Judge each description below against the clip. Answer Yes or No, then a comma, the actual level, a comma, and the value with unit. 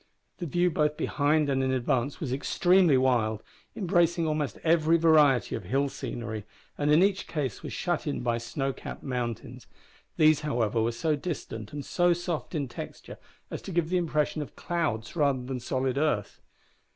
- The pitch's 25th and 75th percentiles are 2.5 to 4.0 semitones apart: No, average, 4.6 semitones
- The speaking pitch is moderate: Yes, medium, 145 Hz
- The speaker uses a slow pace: No, average, 175 wpm